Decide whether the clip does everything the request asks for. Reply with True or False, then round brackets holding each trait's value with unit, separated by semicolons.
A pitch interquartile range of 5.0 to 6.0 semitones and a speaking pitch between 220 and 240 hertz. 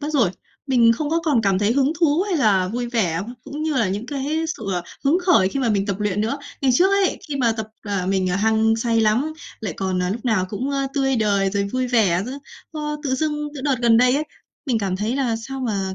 True (5.5 semitones; 235 Hz)